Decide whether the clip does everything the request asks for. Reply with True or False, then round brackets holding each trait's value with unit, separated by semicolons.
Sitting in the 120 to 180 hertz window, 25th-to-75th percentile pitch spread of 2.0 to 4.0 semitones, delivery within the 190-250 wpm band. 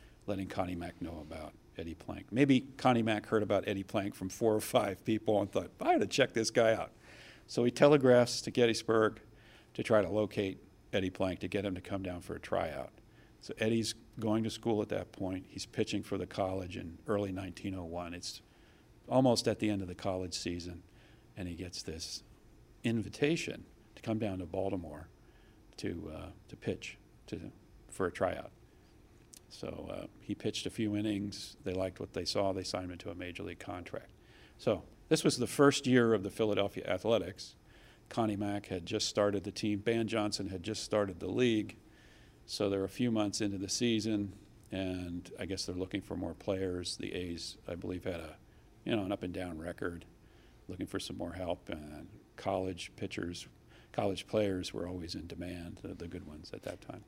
False (100 Hz; 3.2 semitones; 195 wpm)